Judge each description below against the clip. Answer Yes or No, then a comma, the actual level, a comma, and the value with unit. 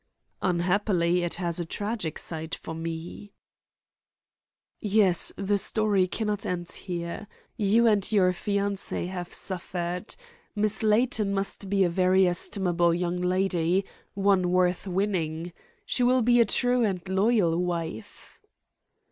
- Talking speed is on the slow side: Yes, slow, 125 wpm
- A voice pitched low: No, medium, 185 Hz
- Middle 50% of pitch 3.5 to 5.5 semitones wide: No, average, 2.8 semitones